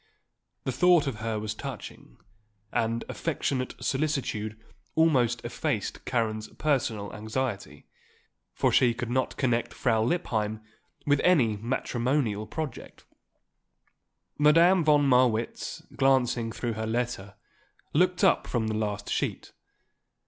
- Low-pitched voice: Yes, low, 120 Hz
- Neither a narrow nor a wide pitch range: Yes, average, 4.5 semitones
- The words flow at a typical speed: No, slow, 110 wpm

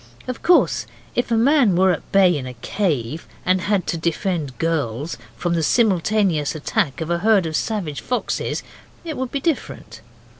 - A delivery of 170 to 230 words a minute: Yes, average, 175 wpm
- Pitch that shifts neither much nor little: No, wide, 6.2 semitones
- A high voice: No, medium, 175 Hz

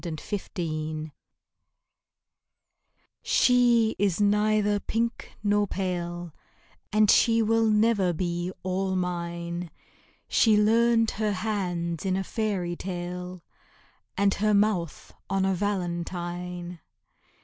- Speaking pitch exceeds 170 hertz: Yes, high, 190 Hz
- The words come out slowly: Yes, slow, 100 wpm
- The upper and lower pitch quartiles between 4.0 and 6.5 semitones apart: No, average, 3.3 semitones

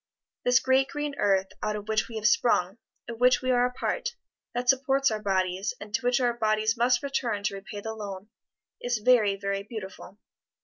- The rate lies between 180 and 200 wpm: Yes, average, 195 wpm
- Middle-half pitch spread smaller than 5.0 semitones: Yes, average, 3.5 semitones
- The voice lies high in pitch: Yes, high, 220 Hz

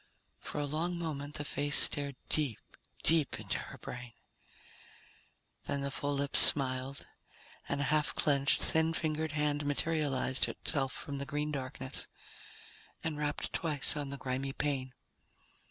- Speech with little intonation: Yes, narrow, 1.8 semitones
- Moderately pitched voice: Yes, medium, 145 Hz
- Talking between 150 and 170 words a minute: No, average, 140 wpm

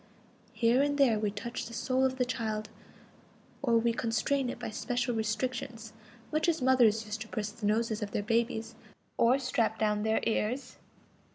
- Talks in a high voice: Yes, high, 230 Hz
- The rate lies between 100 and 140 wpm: No, average, 175 wpm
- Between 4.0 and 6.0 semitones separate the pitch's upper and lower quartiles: No, average, 2.7 semitones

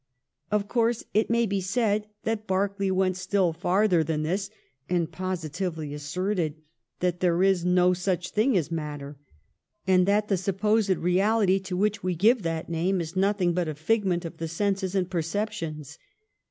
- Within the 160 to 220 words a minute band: Yes, average, 165 wpm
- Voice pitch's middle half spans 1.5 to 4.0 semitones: Yes, average, 3.1 semitones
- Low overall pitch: No, medium, 185 Hz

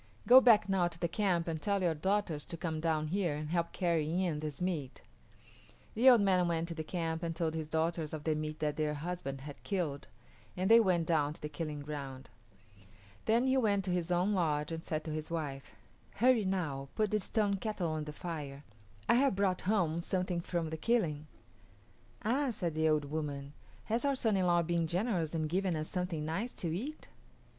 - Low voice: No, medium, 170 Hz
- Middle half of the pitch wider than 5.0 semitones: No, average, 3.9 semitones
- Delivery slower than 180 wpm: No, fast, 205 wpm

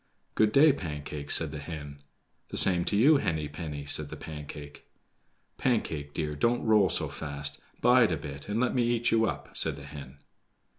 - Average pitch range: No, wide, 7.4 semitones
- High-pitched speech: No, very low, 80 Hz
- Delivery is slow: No, average, 185 wpm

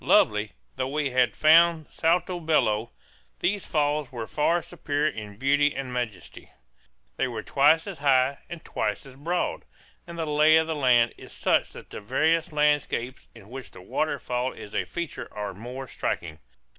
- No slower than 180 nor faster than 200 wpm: No, average, 170 wpm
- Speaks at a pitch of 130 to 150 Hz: Yes, medium, 140 Hz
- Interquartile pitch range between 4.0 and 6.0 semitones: Yes, average, 4.6 semitones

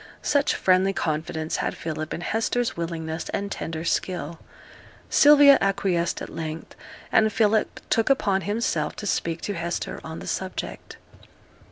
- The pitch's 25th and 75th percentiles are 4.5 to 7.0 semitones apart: Yes, average, 4.8 semitones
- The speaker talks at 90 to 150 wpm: Yes, average, 140 wpm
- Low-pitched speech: No, medium, 185 Hz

